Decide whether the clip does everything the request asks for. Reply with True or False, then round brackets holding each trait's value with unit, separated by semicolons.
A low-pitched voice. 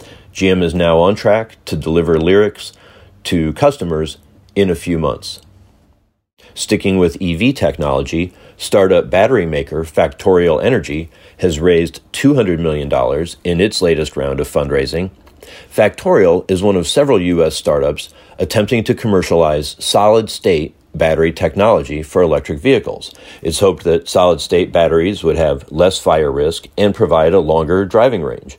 True (90 Hz)